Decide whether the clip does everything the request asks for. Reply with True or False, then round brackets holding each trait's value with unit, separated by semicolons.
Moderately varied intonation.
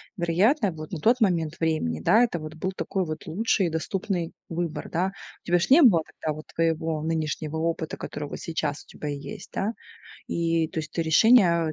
True (3.0 semitones)